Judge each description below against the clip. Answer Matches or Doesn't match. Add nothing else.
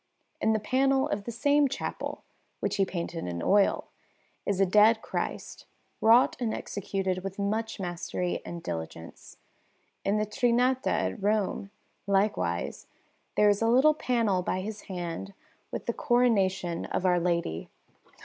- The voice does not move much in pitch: Doesn't match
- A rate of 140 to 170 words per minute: Matches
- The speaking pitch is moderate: Doesn't match